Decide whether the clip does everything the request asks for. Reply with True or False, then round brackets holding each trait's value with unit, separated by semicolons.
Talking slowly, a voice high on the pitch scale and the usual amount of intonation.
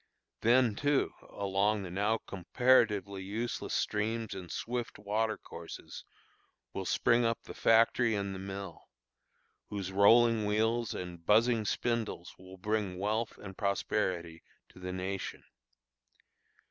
False (120 wpm; 105 Hz; 3.1 semitones)